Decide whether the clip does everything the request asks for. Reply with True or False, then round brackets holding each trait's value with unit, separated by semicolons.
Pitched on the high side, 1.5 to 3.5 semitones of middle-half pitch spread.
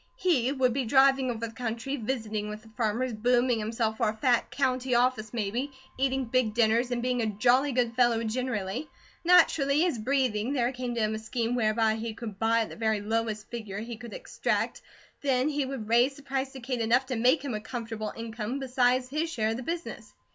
True (240 Hz; 2.9 semitones)